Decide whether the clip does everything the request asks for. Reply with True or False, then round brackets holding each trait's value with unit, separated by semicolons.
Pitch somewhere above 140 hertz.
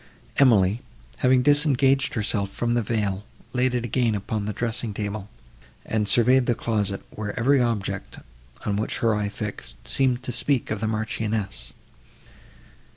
False (110 Hz)